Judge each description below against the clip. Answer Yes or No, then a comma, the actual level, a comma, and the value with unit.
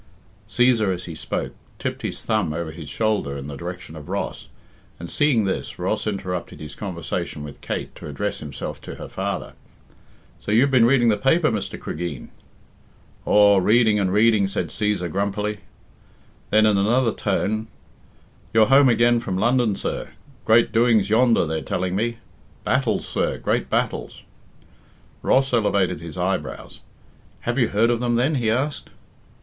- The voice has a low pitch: Yes, low, 105 Hz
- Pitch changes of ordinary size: Yes, average, 4.4 semitones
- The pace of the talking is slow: No, average, 155 wpm